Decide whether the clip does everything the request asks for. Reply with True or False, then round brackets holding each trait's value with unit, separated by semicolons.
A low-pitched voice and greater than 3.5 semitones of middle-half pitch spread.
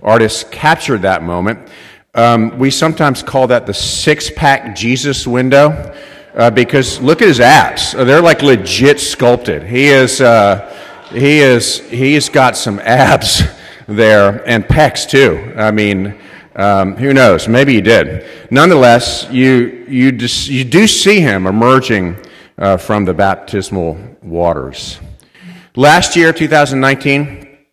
True (125 Hz; 5.0 semitones)